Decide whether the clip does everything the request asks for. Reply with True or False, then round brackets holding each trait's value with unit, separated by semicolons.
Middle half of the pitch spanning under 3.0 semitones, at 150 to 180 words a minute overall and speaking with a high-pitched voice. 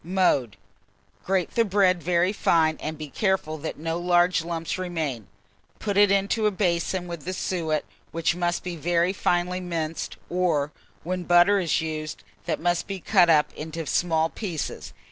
False (2.4 semitones; 165 wpm; 175 Hz)